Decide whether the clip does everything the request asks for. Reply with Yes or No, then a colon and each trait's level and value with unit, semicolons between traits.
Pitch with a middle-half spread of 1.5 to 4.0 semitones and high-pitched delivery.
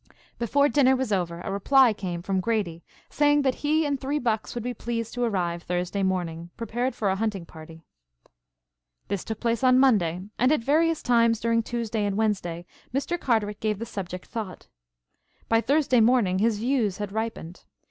No: average, 4.9 semitones; high, 225 Hz